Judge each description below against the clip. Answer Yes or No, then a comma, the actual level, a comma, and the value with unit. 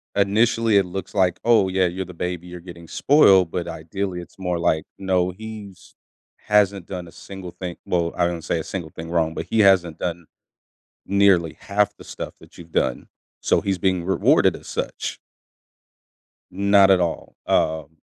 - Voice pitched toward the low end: Yes, very low, 90 Hz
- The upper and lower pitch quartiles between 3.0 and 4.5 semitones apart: No, narrow, 2.4 semitones